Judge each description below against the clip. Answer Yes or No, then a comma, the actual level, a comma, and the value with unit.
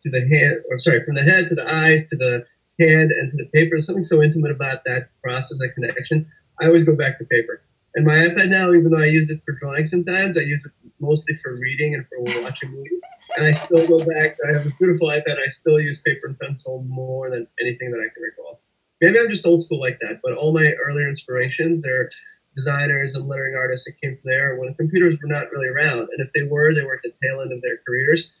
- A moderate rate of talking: No, fast, 240 wpm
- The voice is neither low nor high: Yes, medium, 150 Hz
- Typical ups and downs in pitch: Yes, average, 3.6 semitones